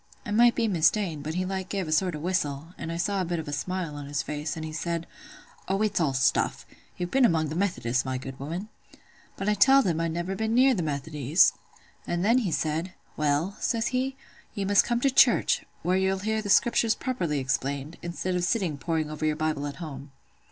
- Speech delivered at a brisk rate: Yes, fast, 220 wpm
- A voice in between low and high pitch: Yes, medium, 170 Hz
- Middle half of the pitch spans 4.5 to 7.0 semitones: Yes, average, 4.9 semitones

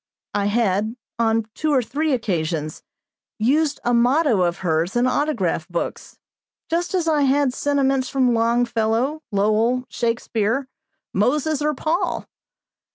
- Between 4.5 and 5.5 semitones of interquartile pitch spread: Yes, average, 5.1 semitones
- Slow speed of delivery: Yes, slow, 125 wpm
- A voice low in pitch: No, high, 240 Hz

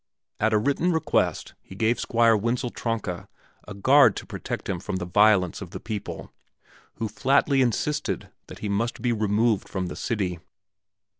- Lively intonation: No, average, 3.3 semitones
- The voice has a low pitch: Yes, low, 110 Hz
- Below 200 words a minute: Yes, average, 165 wpm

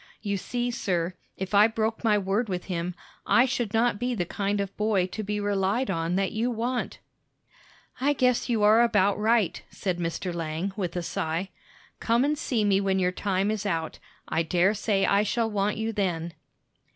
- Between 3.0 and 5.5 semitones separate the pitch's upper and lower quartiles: Yes, average, 3.3 semitones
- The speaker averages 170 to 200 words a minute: Yes, average, 190 wpm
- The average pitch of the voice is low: No, high, 205 Hz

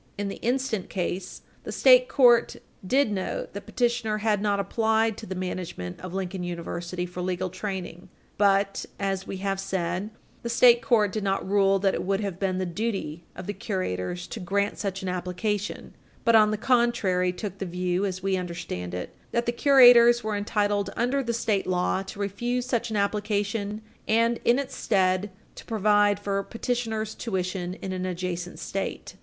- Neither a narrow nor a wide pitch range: Yes, average, 3.2 semitones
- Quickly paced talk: No, average, 180 wpm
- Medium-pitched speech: No, high, 200 Hz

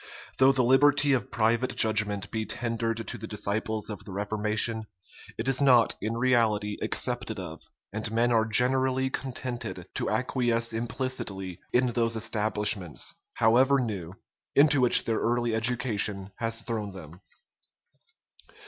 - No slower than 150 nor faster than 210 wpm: No, slow, 135 wpm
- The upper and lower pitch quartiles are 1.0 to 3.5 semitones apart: Yes, average, 2.8 semitones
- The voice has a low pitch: Yes, low, 115 Hz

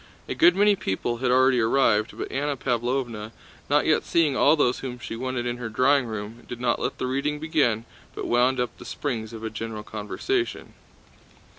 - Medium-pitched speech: No, low, 125 Hz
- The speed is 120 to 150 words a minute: No, average, 190 wpm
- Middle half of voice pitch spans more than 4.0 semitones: No, average, 3.4 semitones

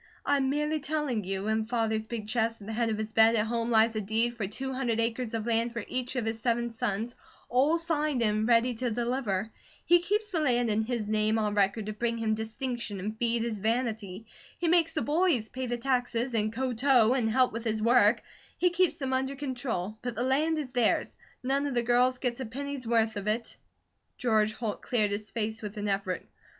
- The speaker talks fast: Yes, fast, 220 wpm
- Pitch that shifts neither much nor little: Yes, average, 3.0 semitones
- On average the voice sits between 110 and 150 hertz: No, high, 235 Hz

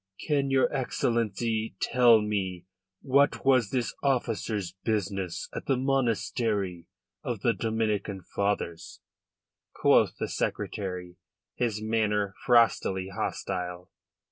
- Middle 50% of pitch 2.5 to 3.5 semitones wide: No, average, 4.0 semitones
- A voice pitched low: Yes, low, 110 Hz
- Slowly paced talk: Yes, slow, 100 wpm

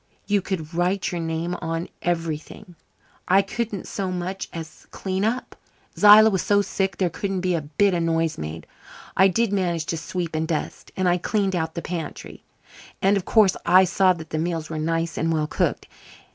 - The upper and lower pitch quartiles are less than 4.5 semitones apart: Yes, average, 2.9 semitones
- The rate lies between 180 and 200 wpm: Yes, average, 190 wpm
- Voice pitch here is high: No, medium, 175 Hz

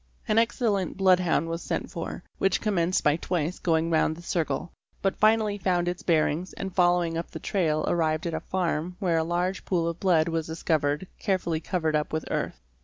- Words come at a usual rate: Yes, average, 190 wpm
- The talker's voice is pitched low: No, medium, 175 Hz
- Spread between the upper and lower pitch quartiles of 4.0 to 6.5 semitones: No, narrow, 2.6 semitones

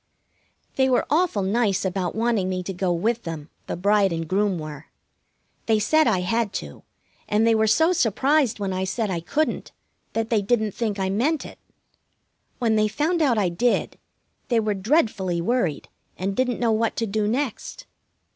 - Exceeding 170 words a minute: Yes, average, 180 wpm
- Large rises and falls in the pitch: No, average, 4.1 semitones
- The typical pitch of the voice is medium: No, high, 215 Hz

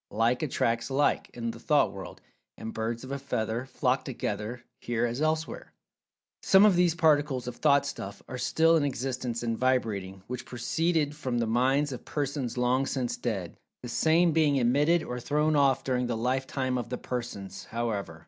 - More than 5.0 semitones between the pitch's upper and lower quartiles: No, average, 3.6 semitones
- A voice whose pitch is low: Yes, low, 125 Hz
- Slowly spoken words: No, average, 175 wpm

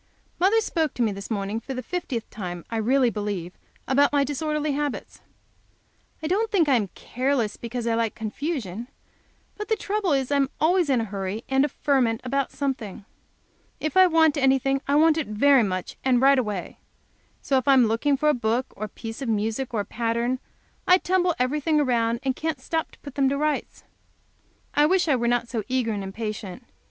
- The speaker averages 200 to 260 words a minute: Yes, fast, 205 wpm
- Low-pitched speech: No, very high, 260 Hz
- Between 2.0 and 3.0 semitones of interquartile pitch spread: No, average, 4.7 semitones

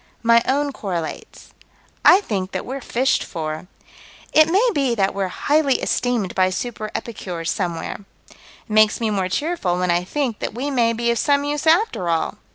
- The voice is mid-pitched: No, high, 230 Hz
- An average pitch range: No, wide, 7.2 semitones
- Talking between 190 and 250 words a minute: No, average, 175 wpm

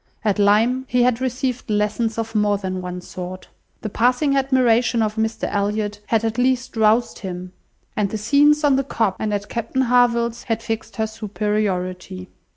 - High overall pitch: Yes, high, 220 Hz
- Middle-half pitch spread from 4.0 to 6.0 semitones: No, average, 3.0 semitones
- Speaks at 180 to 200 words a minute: No, average, 170 wpm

